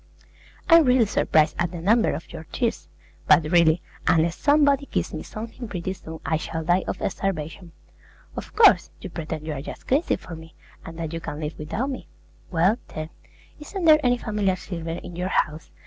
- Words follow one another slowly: No, average, 185 wpm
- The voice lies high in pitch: No, medium, 175 Hz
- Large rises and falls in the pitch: Yes, wide, 6.3 semitones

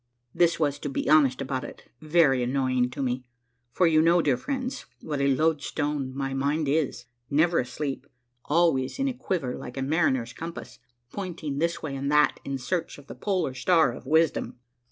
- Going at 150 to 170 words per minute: No, average, 180 wpm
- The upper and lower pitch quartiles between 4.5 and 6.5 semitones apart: No, average, 3.7 semitones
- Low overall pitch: No, medium, 145 Hz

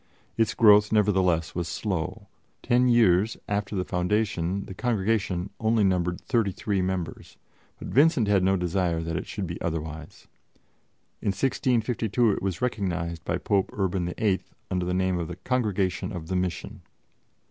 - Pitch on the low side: Yes, very low, 95 Hz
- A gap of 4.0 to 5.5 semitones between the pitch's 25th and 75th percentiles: No, average, 3.4 semitones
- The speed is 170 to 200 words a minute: No, average, 155 wpm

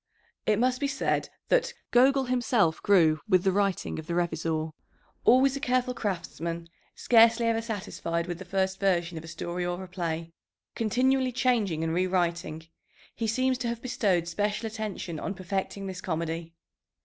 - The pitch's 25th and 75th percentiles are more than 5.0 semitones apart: Yes, wide, 5.6 semitones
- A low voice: No, high, 190 Hz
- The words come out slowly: No, average, 160 wpm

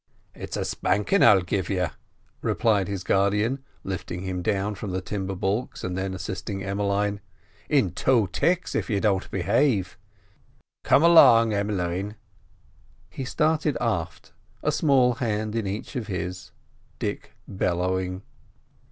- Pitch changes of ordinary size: Yes, average, 3.4 semitones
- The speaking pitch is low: Yes, low, 100 Hz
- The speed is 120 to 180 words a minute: Yes, slow, 135 wpm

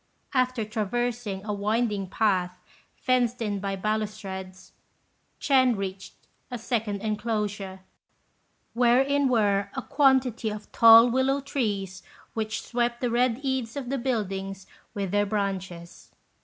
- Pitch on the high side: Yes, high, 220 Hz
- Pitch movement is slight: No, average, 3.7 semitones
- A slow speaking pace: Yes, slow, 120 wpm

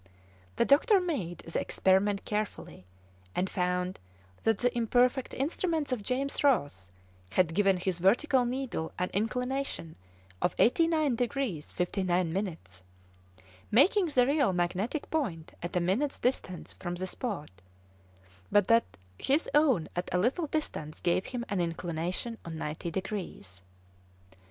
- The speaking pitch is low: No, high, 205 Hz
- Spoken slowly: Yes, slow, 130 wpm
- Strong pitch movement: Yes, wide, 7.0 semitones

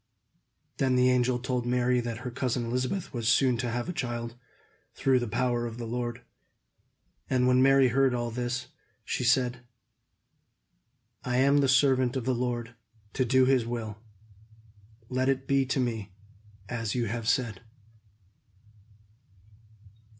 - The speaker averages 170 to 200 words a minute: No, average, 145 wpm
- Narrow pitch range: Yes, narrow, 1.5 semitones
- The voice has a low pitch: Yes, low, 125 Hz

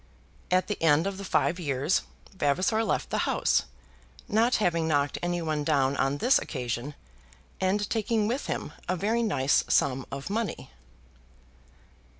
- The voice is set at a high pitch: No, medium, 175 Hz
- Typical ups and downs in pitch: No, wide, 6.5 semitones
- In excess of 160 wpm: No, average, 150 wpm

